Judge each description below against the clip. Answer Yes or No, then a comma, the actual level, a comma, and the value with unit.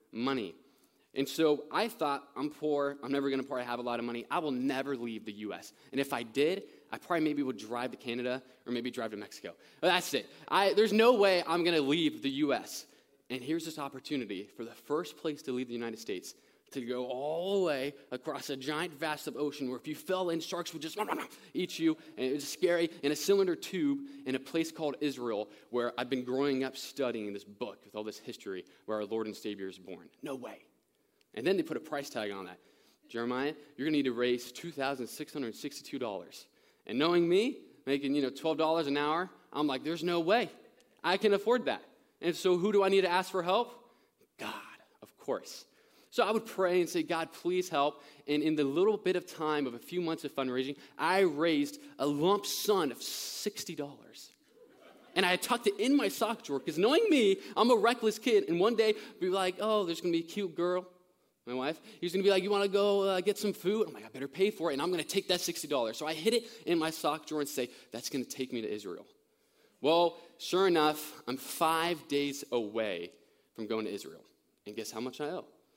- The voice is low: No, medium, 155 Hz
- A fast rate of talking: Yes, fast, 235 wpm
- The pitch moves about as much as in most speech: No, wide, 6.0 semitones